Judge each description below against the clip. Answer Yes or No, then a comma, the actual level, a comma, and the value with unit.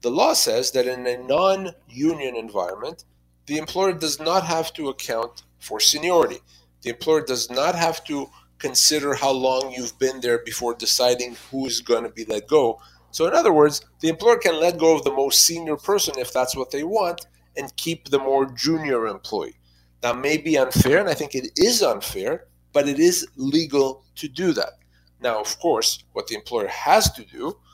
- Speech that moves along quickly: No, average, 195 wpm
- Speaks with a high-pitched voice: No, low, 135 Hz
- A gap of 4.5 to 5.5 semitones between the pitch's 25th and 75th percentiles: Yes, average, 5.2 semitones